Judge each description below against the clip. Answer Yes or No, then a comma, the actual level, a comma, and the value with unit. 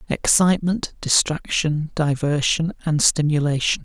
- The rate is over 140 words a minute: No, slow, 80 wpm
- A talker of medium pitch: Yes, medium, 155 Hz